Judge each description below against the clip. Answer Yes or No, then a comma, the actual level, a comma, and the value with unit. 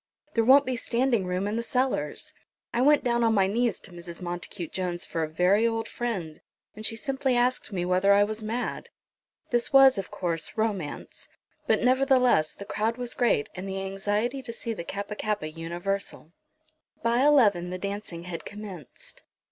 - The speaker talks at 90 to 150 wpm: No, average, 180 wpm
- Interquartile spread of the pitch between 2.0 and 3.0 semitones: No, average, 4.9 semitones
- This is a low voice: No, high, 205 Hz